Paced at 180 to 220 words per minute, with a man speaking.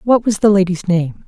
No: fast, 235 wpm; male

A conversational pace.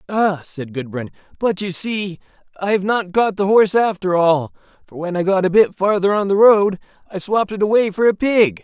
No: fast, 210 wpm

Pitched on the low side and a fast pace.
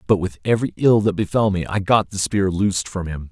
Yes: low, 100 Hz; fast, 255 wpm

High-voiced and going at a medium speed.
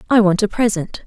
No: high, 205 Hz; fast, 225 wpm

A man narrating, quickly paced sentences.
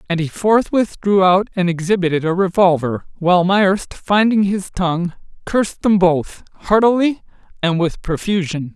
No: male; average, 145 wpm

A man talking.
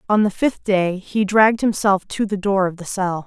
No: female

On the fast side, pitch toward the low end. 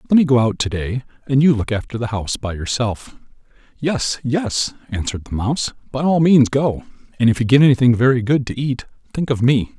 Yes: fast, 210 wpm; low, 125 Hz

